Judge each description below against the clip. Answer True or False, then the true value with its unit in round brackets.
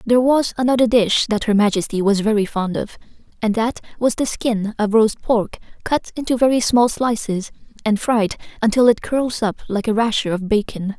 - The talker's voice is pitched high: True (225 Hz)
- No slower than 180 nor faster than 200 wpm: True (190 wpm)